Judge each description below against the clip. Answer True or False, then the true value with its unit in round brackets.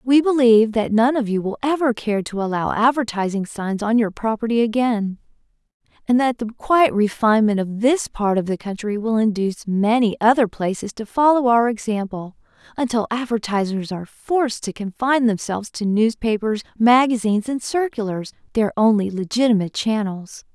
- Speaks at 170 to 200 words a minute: False (155 wpm)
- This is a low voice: False (225 Hz)